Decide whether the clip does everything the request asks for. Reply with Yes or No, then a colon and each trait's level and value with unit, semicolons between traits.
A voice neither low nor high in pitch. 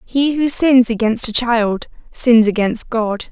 No: high, 235 Hz